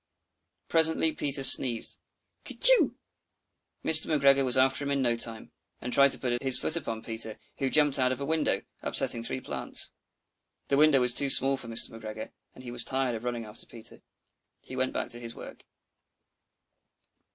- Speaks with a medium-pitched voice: No, low, 130 Hz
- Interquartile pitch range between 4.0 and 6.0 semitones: No, average, 2.8 semitones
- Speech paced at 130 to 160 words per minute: No, average, 175 wpm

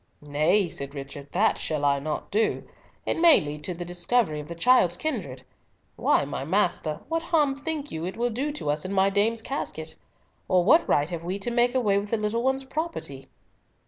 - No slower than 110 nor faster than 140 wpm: No, fast, 205 wpm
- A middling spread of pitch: No, wide, 8.2 semitones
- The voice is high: Yes, high, 195 Hz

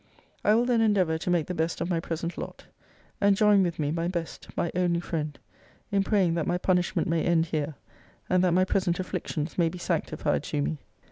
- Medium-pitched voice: Yes, medium, 175 Hz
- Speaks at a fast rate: Yes, fast, 210 wpm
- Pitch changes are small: Yes, narrow, 2.3 semitones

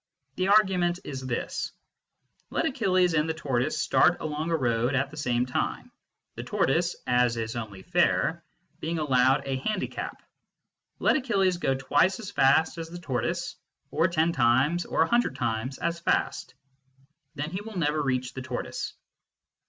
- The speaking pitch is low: No, medium, 150 Hz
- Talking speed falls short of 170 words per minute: Yes, average, 160 wpm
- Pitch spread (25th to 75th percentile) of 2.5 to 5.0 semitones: No, wide, 5.4 semitones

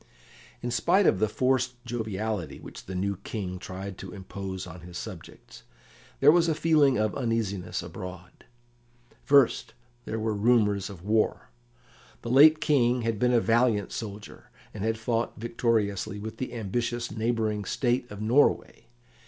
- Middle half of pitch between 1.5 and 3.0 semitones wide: No, average, 3.4 semitones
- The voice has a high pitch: No, low, 110 Hz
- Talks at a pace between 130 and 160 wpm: Yes, average, 150 wpm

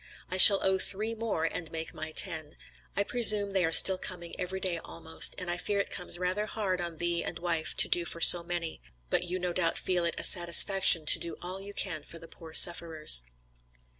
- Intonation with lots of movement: No, narrow, 2.4 semitones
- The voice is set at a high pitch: No, medium, 175 Hz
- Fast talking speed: Yes, fast, 220 wpm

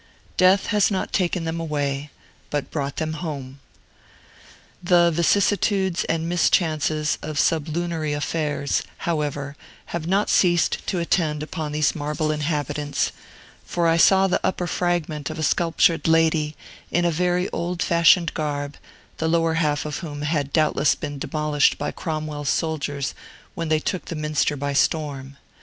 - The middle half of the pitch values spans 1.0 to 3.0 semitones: Yes, narrow, 2.5 semitones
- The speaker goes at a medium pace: Yes, average, 145 wpm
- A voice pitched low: No, medium, 155 Hz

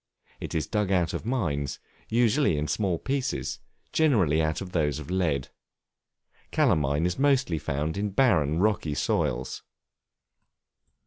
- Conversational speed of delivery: No, slow, 130 wpm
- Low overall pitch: Yes, very low, 90 Hz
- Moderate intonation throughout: No, wide, 6.7 semitones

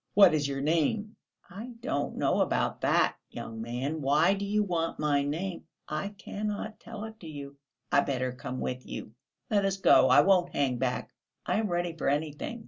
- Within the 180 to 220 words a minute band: Yes, average, 185 wpm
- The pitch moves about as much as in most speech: No, wide, 6.1 semitones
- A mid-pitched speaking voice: Yes, medium, 165 Hz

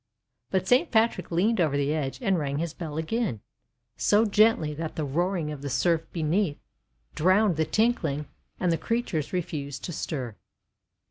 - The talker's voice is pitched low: No, medium, 165 Hz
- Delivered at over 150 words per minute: Yes, average, 160 wpm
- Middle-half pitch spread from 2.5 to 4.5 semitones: No, average, 4.9 semitones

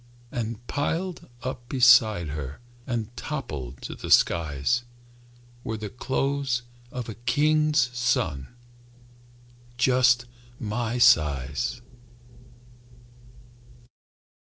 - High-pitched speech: No, low, 120 Hz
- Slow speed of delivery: Yes, slow, 80 wpm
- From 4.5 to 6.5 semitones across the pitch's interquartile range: No, average, 3.8 semitones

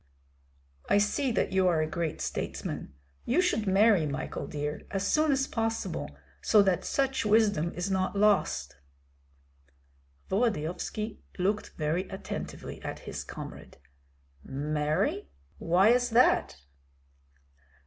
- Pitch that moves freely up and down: Yes, wide, 5.9 semitones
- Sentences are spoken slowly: Yes, slow, 120 wpm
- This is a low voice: No, high, 195 Hz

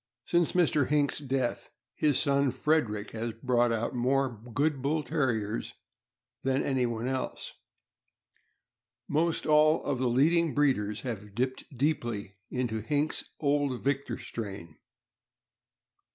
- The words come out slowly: Yes, slow, 115 wpm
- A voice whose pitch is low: Yes, low, 130 Hz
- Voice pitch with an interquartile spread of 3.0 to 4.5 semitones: Yes, average, 4.0 semitones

